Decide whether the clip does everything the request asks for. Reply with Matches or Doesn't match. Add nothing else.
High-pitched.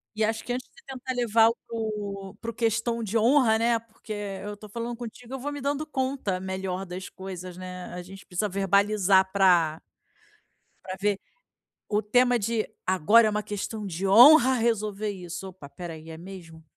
Matches